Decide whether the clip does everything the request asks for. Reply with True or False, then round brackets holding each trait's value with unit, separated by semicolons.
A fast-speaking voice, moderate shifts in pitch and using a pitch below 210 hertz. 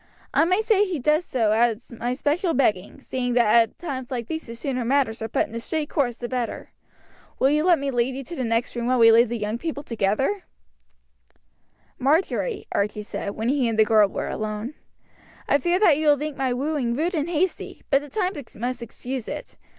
False (215 wpm; 4.7 semitones; 255 Hz)